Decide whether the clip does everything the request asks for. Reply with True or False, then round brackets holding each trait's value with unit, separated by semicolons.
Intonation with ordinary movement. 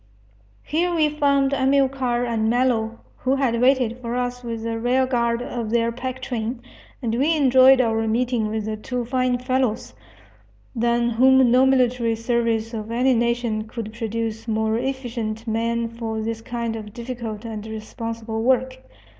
False (2.2 semitones)